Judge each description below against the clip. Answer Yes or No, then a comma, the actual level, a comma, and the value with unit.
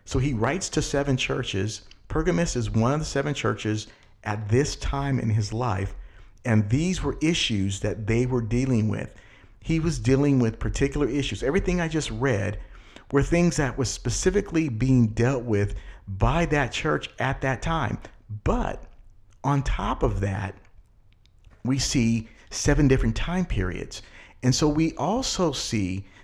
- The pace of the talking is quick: No, average, 155 wpm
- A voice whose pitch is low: Yes, low, 120 Hz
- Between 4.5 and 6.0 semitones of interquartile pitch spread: Yes, average, 5.2 semitones